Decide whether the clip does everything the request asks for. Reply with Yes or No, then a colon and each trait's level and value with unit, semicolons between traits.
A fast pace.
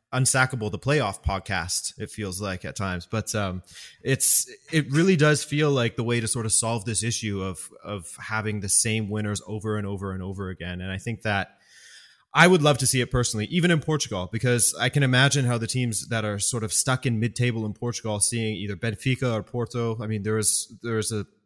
Yes: fast, 225 wpm